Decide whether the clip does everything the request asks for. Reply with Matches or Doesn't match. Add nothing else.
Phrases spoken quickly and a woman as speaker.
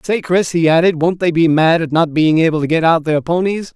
Doesn't match